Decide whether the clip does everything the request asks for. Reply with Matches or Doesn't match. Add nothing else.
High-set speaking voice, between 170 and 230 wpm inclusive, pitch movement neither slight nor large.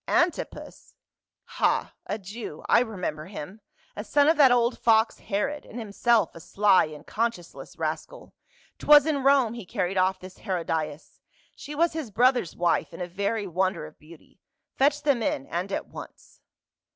Doesn't match